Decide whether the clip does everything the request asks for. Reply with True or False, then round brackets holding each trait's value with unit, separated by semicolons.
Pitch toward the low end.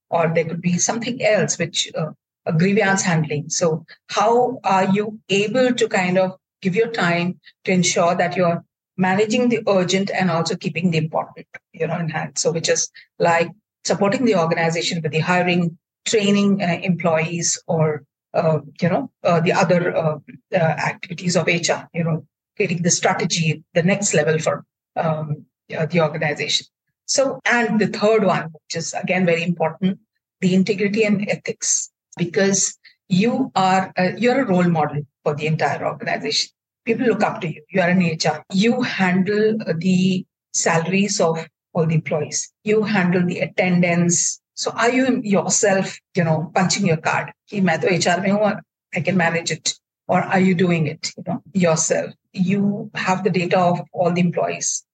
False (180 Hz)